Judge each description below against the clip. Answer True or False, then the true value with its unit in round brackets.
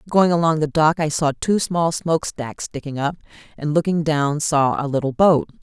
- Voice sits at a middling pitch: True (155 Hz)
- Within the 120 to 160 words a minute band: False (190 wpm)